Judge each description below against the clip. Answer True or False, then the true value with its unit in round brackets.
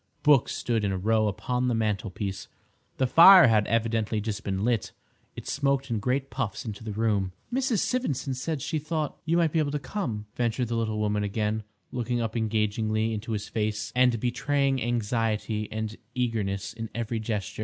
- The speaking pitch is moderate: False (115 Hz)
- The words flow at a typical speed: True (180 wpm)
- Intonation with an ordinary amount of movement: True (3.1 semitones)